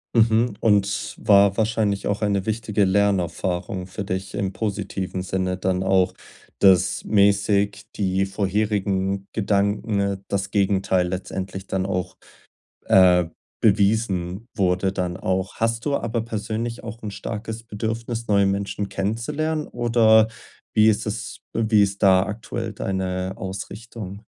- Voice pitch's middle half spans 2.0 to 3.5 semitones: Yes, narrow, 2.6 semitones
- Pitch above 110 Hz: No, low, 100 Hz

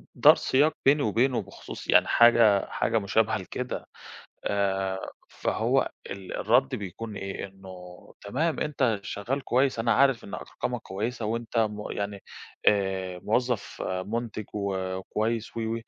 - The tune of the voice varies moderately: Yes, average, 3.3 semitones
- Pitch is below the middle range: Yes, low, 110 Hz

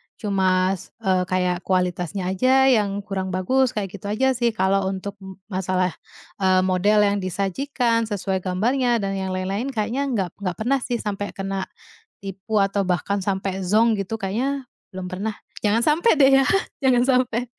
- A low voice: No, high, 200 Hz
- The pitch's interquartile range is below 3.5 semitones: No, average, 3.8 semitones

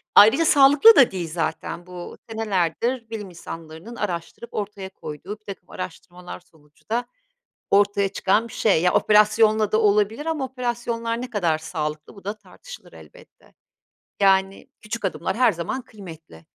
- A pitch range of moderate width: Yes, average, 4.6 semitones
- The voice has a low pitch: No, high, 205 Hz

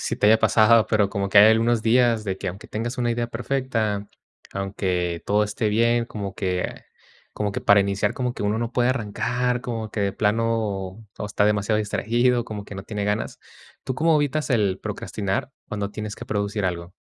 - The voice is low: Yes, low, 105 Hz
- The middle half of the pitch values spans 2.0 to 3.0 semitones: Yes, narrow, 2.6 semitones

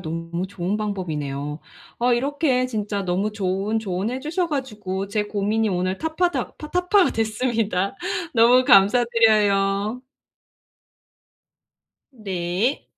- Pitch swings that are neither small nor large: Yes, average, 4.7 semitones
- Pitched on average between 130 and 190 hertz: No, high, 210 Hz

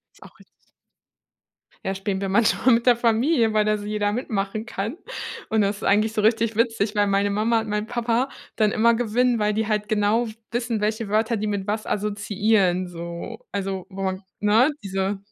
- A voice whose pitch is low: No, high, 215 Hz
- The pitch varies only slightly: Yes, narrow, 2.1 semitones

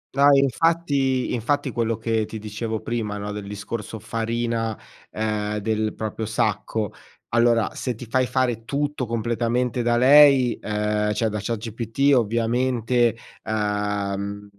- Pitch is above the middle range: No, low, 115 Hz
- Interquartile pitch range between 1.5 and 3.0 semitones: Yes, average, 2.7 semitones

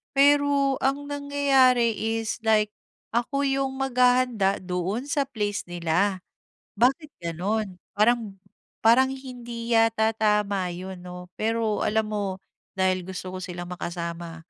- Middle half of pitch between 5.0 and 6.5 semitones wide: Yes, wide, 5.4 semitones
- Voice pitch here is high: Yes, high, 220 Hz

